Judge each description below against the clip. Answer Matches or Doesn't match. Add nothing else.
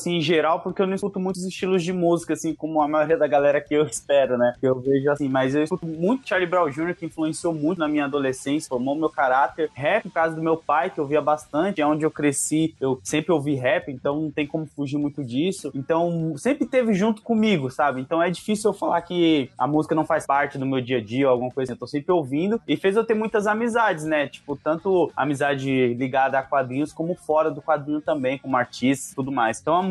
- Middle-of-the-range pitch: Matches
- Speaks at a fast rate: Matches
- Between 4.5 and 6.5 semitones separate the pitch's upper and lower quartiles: Doesn't match